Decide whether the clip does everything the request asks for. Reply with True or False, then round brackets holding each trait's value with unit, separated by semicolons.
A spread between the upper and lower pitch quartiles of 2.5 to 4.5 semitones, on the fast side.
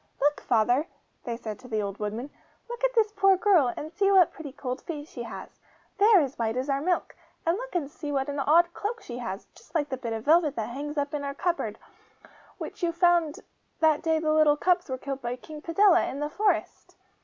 False (5.0 semitones; 235 wpm)